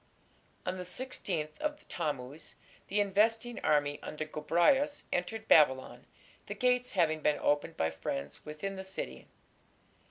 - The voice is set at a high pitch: No, medium, 175 Hz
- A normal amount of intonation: No, wide, 6.5 semitones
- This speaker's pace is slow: Yes, slow, 130 wpm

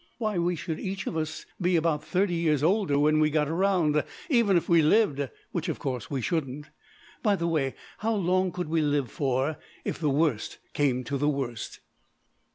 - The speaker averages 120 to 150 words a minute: No, average, 190 wpm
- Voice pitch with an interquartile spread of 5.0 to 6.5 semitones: No, average, 3.8 semitones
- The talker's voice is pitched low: No, medium, 155 Hz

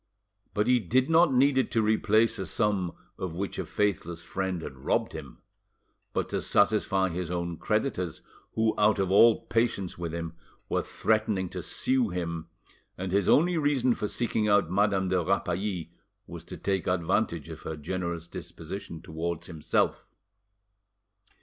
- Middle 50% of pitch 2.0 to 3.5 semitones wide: No, average, 4.1 semitones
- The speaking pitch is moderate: No, very low, 95 Hz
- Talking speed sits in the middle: Yes, average, 155 wpm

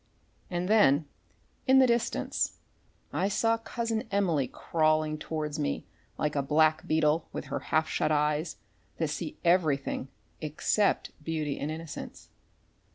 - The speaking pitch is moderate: Yes, medium, 155 Hz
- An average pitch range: Yes, average, 3.5 semitones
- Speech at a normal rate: No, slow, 130 wpm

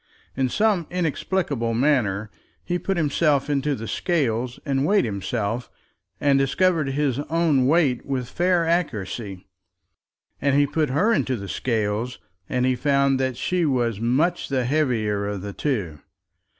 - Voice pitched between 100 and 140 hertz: Yes, low, 135 Hz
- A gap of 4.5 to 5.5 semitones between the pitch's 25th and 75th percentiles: Yes, average, 5.0 semitones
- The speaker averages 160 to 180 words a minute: No, average, 145 wpm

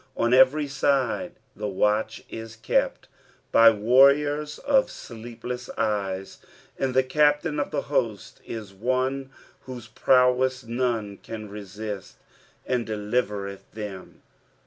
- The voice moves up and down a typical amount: Yes, average, 3.9 semitones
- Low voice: Yes, low, 120 Hz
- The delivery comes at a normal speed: No, slow, 115 wpm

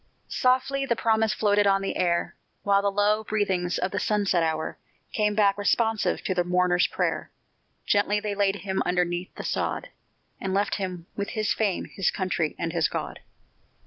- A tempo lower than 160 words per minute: No, average, 175 wpm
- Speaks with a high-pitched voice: Yes, high, 200 Hz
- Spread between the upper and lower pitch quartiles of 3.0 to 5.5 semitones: No, narrow, 2.6 semitones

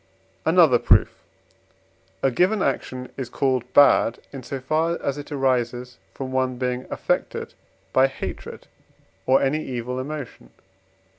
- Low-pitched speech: Yes, low, 130 Hz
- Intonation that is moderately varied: No, narrow, 1.9 semitones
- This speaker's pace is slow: Yes, slow, 130 wpm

